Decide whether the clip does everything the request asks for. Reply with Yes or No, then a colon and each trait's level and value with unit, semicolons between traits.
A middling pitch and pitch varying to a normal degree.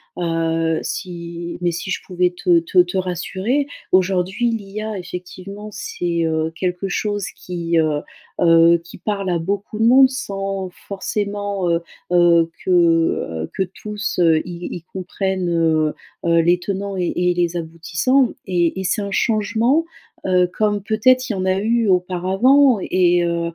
Yes: medium, 180 Hz; average, 3.1 semitones